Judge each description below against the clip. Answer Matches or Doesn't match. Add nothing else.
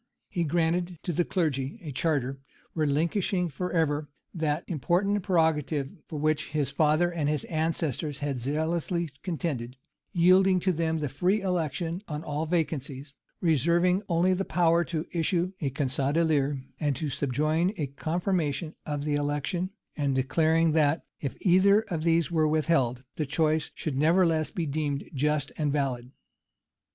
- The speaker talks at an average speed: Matches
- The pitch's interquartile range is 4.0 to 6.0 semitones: Doesn't match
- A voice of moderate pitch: Matches